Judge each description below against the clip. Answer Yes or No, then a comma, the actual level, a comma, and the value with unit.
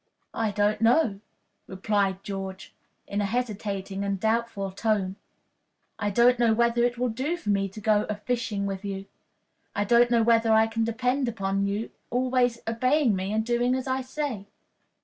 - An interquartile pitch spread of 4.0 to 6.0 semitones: No, average, 3.2 semitones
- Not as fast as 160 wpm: No, average, 170 wpm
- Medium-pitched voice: No, high, 220 Hz